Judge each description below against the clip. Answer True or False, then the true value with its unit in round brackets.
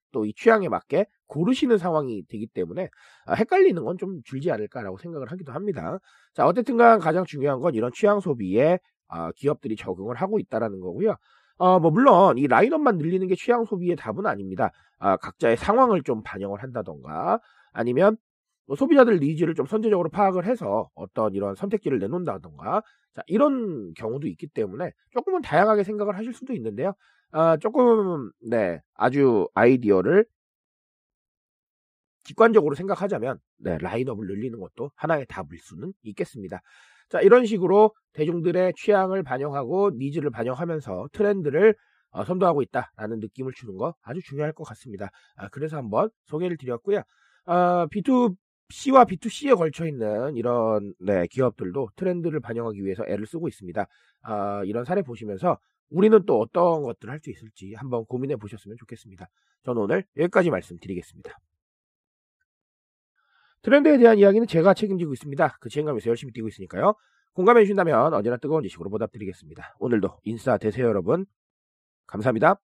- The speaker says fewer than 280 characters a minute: False (380 characters per minute)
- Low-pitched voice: False (165 Hz)